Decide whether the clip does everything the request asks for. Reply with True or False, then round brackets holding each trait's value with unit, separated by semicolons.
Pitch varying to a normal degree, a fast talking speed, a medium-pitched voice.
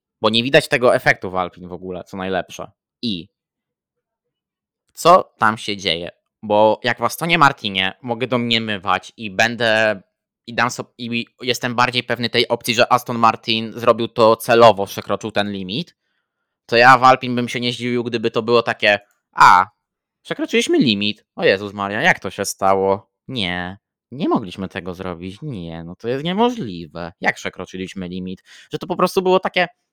False (4.4 semitones; 170 wpm; 115 Hz)